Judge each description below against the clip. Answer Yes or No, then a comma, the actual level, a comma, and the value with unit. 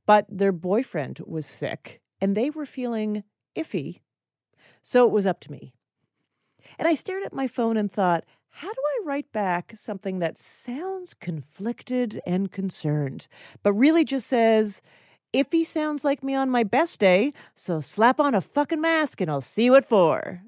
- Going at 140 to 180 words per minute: Yes, average, 170 wpm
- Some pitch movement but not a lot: No, wide, 6.4 semitones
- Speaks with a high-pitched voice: Yes, high, 220 Hz